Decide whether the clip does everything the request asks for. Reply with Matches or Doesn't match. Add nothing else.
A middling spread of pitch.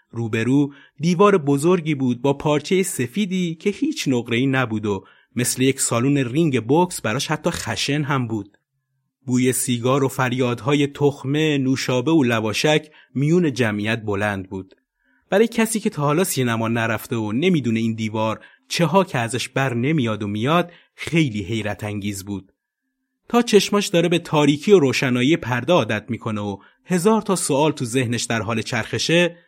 Doesn't match